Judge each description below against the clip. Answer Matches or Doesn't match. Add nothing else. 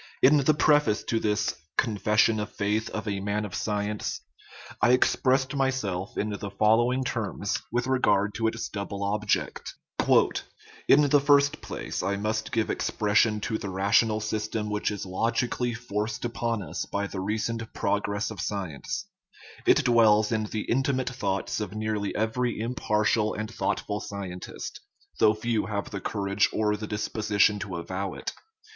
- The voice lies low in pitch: Matches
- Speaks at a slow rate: Doesn't match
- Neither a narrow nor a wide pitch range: Doesn't match